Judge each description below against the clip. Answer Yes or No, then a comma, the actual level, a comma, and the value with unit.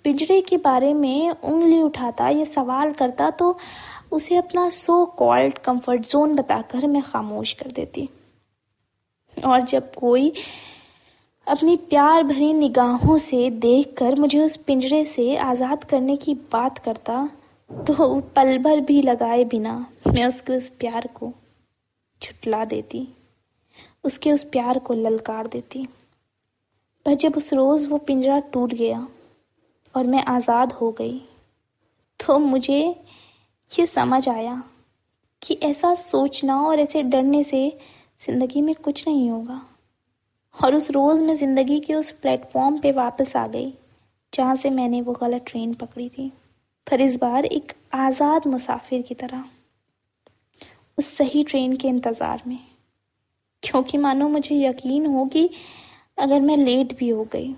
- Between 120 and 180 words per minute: Yes, average, 140 wpm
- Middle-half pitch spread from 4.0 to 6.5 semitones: No, average, 3.1 semitones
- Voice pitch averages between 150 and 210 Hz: No, very high, 270 Hz